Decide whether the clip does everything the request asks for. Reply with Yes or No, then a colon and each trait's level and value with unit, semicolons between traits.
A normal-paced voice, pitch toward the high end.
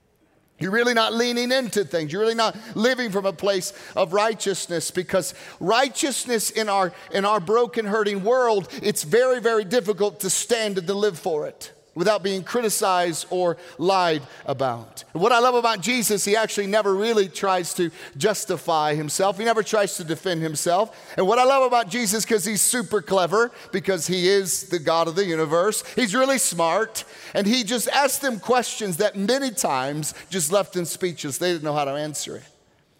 Yes: average, 185 wpm; high, 200 Hz